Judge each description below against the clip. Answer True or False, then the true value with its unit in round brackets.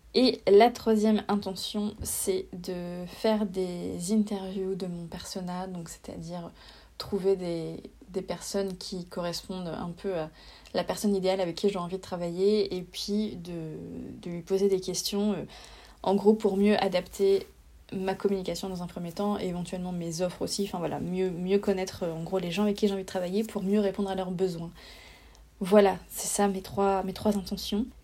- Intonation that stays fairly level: True (2.2 semitones)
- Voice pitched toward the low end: False (190 Hz)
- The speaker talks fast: False (180 wpm)